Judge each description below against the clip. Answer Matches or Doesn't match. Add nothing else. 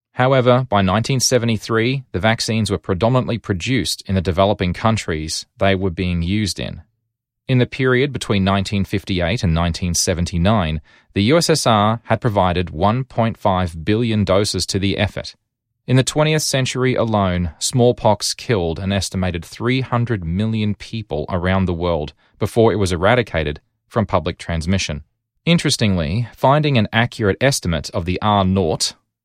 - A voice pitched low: Matches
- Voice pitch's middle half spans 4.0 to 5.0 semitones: Matches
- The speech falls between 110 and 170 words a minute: Matches